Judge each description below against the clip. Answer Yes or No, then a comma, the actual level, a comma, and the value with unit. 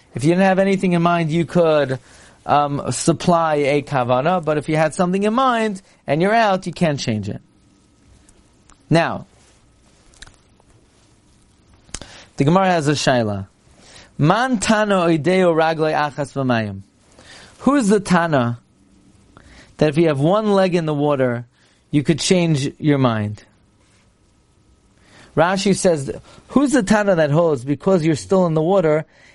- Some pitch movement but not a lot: No, wide, 7.3 semitones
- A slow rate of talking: Yes, slow, 130 wpm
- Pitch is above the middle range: No, medium, 155 Hz